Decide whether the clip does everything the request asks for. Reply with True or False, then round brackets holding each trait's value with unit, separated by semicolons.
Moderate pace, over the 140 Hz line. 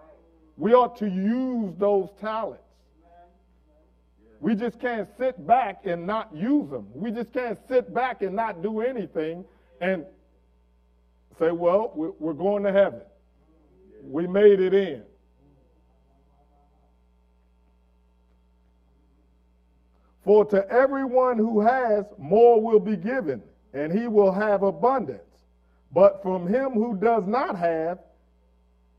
False (115 wpm; 190 Hz)